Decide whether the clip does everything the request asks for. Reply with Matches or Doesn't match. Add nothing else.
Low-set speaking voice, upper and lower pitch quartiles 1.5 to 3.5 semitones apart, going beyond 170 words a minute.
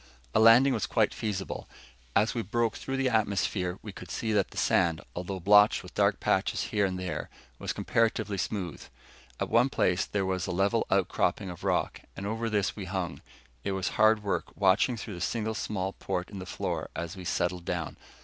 Matches